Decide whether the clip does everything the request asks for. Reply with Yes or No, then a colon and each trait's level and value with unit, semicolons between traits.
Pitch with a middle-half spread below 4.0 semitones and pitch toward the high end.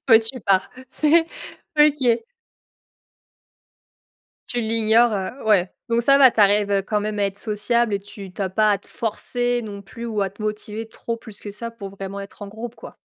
Yes: average, 2.8 semitones; high, 215 Hz